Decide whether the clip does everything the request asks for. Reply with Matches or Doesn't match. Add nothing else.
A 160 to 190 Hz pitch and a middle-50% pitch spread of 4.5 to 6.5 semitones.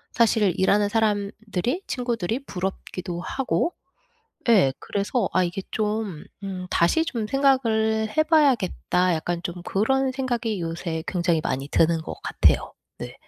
Doesn't match